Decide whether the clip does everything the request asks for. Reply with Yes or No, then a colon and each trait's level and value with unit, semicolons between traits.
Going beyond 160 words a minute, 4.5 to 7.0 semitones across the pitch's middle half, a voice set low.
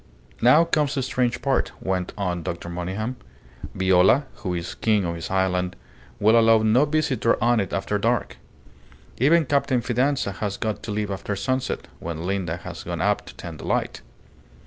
Yes: average, 170 wpm; wide, 5.6 semitones; low, 105 Hz